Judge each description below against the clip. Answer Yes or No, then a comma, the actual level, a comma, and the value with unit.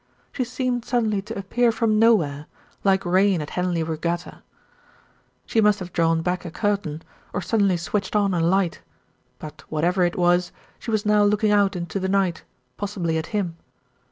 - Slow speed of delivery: No, average, 170 wpm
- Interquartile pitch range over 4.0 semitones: No, average, 3.4 semitones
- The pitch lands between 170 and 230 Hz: Yes, high, 190 Hz